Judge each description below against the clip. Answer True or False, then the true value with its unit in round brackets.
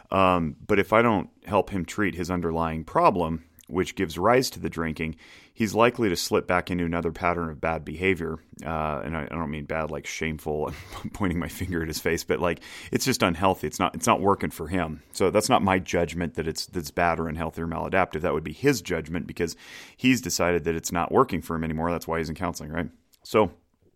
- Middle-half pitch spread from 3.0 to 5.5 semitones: False (2.4 semitones)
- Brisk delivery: True (230 wpm)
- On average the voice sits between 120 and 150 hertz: False (85 Hz)